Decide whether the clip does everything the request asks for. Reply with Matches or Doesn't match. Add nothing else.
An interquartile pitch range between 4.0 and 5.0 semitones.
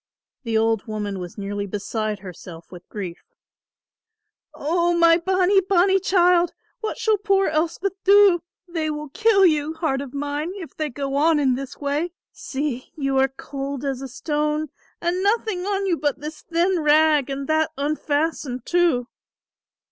Matches